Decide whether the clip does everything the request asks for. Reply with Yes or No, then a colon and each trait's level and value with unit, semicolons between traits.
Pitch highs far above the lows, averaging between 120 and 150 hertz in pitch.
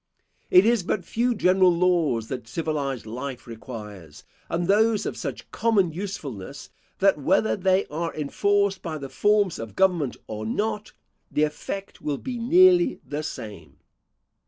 No: wide, 7.1 semitones; medium, 170 Hz